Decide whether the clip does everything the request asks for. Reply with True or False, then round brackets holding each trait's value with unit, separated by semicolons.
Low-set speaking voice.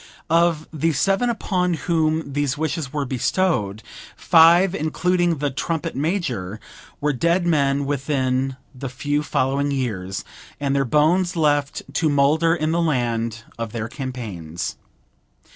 False (145 Hz)